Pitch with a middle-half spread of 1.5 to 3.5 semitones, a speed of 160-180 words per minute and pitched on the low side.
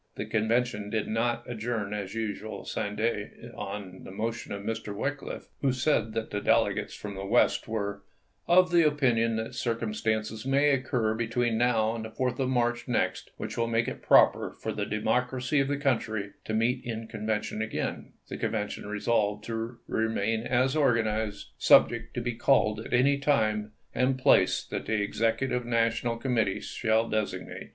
Yes: narrow, 2.4 semitones; average, 175 wpm; low, 115 Hz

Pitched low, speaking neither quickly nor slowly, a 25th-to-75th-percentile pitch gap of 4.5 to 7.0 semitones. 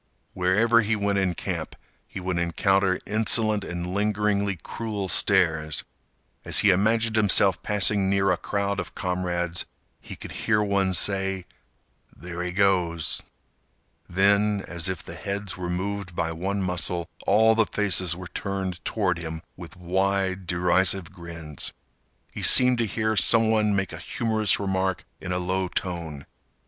No: very low, 95 Hz; average, 150 wpm; narrow, 2.5 semitones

